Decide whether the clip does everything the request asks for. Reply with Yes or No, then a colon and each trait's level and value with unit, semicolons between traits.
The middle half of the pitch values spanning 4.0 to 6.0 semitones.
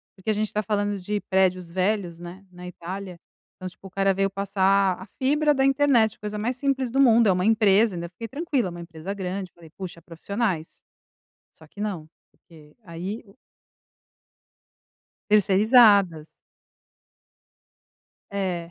No: average, 3.3 semitones